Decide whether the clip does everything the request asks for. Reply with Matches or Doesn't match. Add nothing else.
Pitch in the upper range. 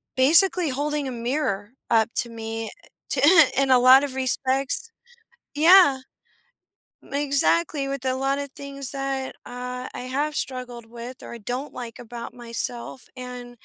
Matches